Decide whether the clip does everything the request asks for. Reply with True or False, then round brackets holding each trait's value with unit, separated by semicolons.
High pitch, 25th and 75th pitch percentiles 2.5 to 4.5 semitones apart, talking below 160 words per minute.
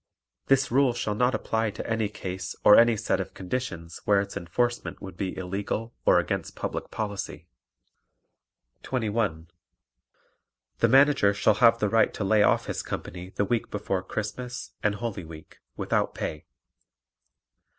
False (105 Hz; 3.7 semitones; 150 wpm)